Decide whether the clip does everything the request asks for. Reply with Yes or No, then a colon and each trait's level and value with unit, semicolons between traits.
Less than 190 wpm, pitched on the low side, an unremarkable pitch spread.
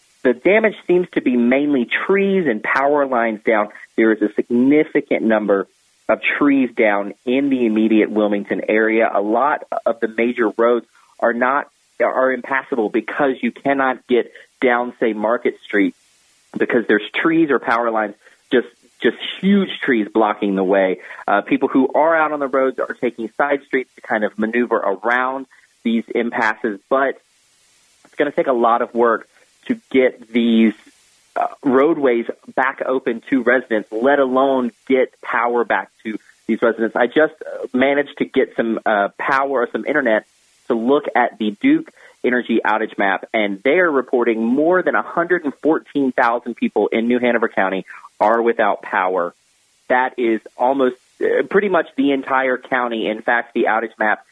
Yes: average, 160 wpm; low, 125 Hz; average, 3.7 semitones